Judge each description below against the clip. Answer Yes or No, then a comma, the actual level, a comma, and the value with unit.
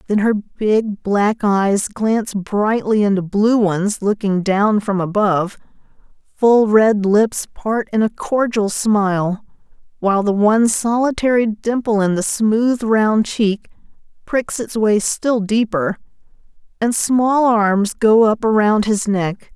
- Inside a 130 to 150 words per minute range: Yes, average, 140 wpm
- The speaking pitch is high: Yes, high, 215 Hz